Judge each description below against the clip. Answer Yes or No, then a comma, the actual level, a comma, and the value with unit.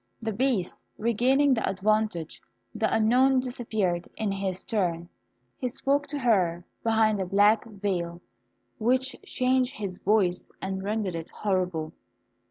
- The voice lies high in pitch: Yes, high, 215 Hz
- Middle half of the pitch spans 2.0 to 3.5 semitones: No, average, 4.7 semitones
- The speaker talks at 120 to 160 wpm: Yes, slow, 135 wpm